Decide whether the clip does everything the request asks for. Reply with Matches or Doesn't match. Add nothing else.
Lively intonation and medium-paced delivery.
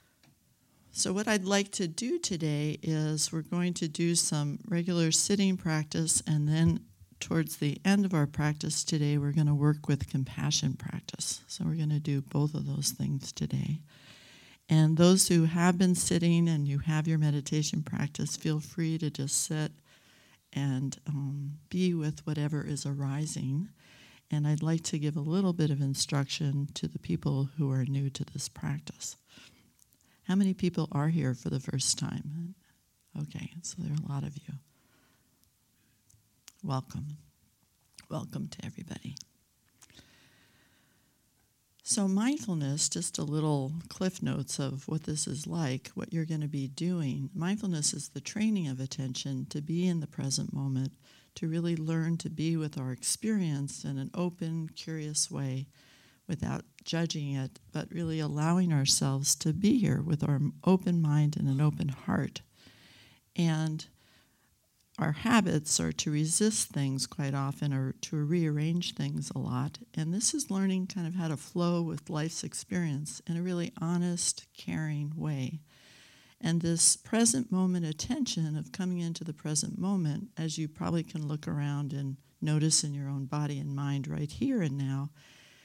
Doesn't match